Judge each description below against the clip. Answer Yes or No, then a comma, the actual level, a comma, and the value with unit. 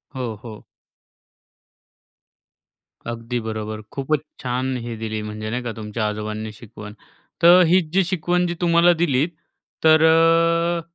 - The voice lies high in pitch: No, low, 130 Hz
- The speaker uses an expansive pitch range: Yes, wide, 7.5 semitones